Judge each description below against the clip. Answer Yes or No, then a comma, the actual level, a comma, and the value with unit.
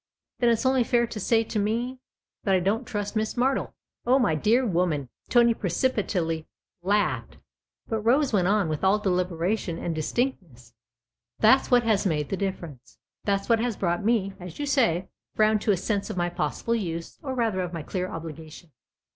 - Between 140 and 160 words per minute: No, fast, 205 wpm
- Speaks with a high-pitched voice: Yes, high, 200 Hz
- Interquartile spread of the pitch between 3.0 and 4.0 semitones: No, average, 5.0 semitones